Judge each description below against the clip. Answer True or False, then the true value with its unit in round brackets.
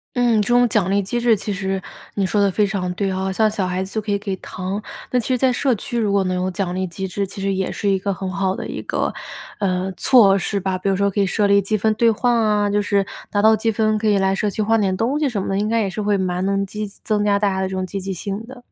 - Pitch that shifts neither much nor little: False (2.1 semitones)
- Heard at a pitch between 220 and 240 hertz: False (200 Hz)